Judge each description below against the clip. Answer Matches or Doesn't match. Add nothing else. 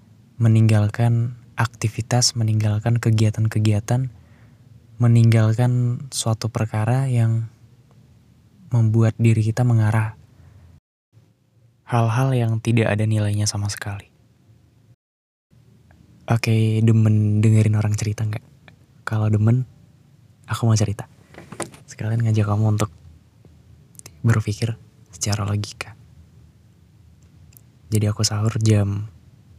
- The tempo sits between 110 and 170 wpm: Doesn't match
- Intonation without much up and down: Matches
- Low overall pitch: Matches